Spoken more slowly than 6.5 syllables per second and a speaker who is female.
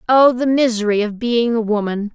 Yes: 5.1 syllables/s; female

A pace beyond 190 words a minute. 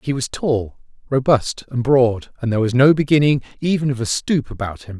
Yes: fast, 205 wpm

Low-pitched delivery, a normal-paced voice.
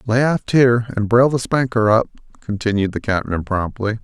Yes: low, 115 Hz; average, 180 wpm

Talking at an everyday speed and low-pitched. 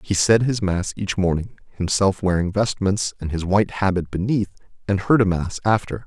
Yes: average, 190 wpm; low, 100 Hz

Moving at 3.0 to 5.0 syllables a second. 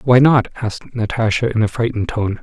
No: 5.9 syllables/s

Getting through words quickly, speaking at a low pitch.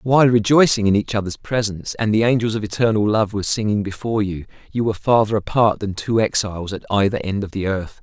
Yes: fast, 215 wpm; low, 105 Hz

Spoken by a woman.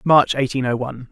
No: male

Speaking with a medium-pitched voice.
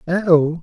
Yes: medium, 170 Hz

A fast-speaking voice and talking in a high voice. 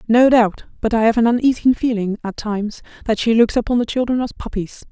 Yes: fast, 220 wpm; high, 230 Hz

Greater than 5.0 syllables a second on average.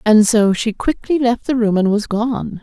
No: 4.4 syllables/s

